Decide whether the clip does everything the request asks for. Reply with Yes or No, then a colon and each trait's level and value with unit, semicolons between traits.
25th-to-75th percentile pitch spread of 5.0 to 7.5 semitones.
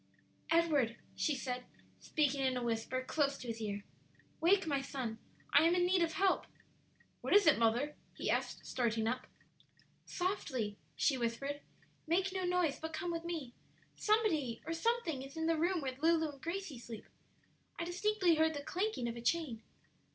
Yes: wide, 5.6 semitones